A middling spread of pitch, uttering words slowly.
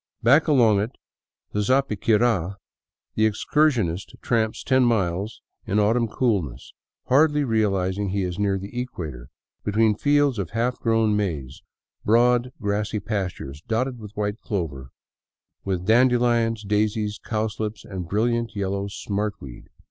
Yes: average, 3.2 semitones; slow, 130 wpm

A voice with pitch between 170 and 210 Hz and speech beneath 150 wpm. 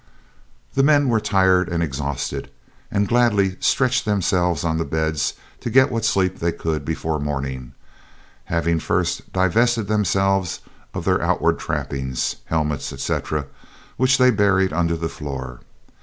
No: very low, 90 Hz; average, 140 wpm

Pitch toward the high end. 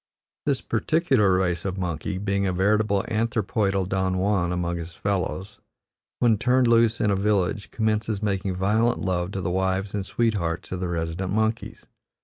No: low, 100 Hz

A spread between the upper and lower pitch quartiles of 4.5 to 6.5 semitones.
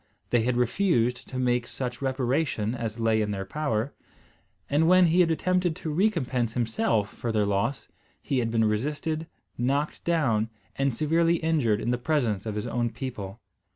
Yes: wide, 5.4 semitones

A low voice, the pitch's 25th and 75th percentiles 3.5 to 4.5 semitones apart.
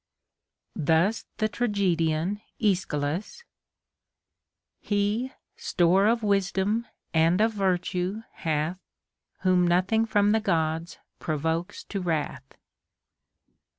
No: medium, 185 Hz; average, 4.0 semitones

